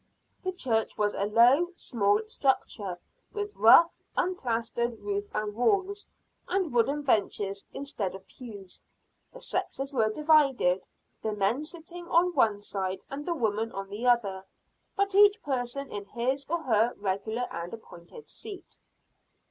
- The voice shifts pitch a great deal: Yes, wide, 7.7 semitones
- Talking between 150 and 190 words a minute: No, average, 140 wpm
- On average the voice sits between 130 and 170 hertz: No, high, 240 Hz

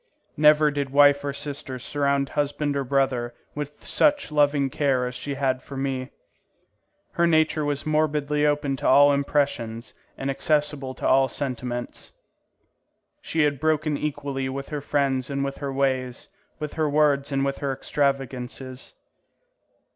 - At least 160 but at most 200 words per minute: No, average, 145 wpm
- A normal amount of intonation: No, narrow, 1.7 semitones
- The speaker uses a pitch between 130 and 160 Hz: Yes, medium, 140 Hz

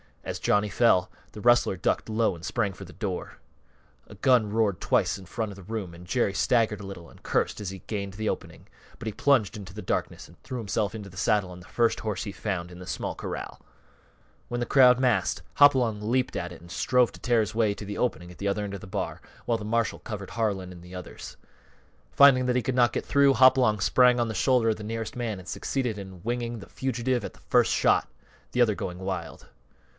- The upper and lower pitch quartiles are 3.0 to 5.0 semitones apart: Yes, average, 3.9 semitones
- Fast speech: Yes, fast, 235 wpm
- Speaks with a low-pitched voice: Yes, low, 110 Hz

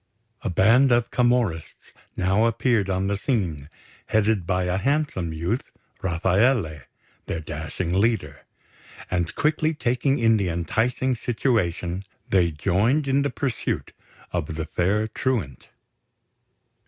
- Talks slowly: Yes, slow, 120 wpm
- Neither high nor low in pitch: No, low, 100 Hz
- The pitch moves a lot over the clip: Yes, wide, 6.0 semitones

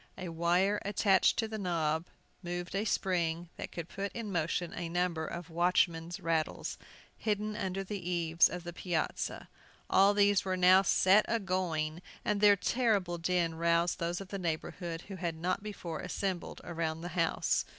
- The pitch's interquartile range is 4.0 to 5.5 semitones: No, narrow, 2.6 semitones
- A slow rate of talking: No, average, 170 wpm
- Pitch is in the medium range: Yes, medium, 180 Hz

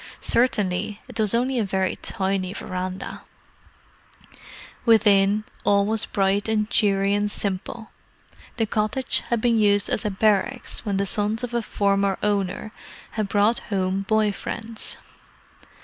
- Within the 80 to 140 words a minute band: Yes, slow, 135 wpm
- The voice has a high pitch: Yes, high, 205 Hz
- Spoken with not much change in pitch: Yes, narrow, 2.0 semitones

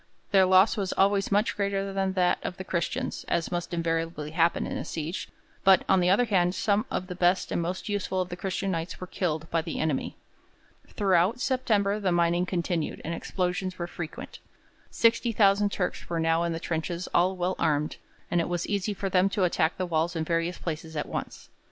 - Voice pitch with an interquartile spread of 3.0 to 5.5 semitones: No, narrow, 2.6 semitones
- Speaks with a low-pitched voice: No, medium, 180 Hz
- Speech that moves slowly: No, fast, 205 wpm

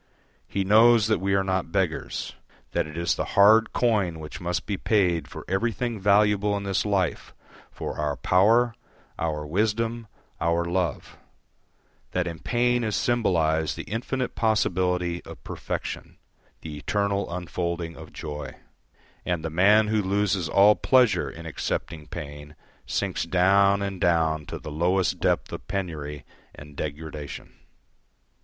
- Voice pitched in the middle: No, very low, 95 Hz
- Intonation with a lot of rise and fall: No, average, 4.2 semitones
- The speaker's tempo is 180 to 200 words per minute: No, average, 140 wpm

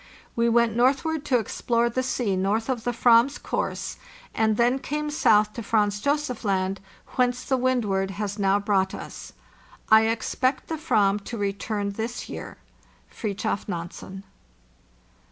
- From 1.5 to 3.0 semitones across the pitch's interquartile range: No, average, 3.7 semitones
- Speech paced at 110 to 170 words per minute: Yes, average, 150 wpm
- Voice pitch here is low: No, high, 225 Hz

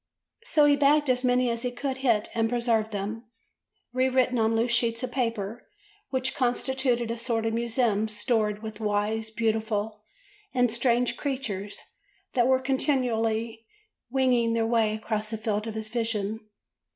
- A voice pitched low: No, high, 230 Hz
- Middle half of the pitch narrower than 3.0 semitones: Yes, narrow, 2.4 semitones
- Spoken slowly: No, average, 160 wpm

